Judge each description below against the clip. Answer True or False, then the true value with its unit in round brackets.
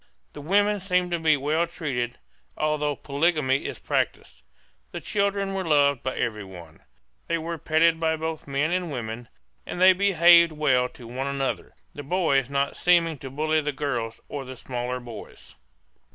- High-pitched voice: False (150 Hz)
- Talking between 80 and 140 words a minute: False (165 wpm)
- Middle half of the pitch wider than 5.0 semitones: False (4.5 semitones)